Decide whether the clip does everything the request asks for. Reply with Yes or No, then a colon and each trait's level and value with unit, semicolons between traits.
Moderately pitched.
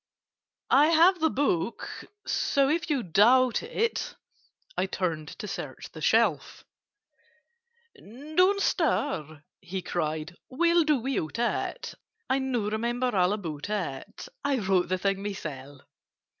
No: high, 225 Hz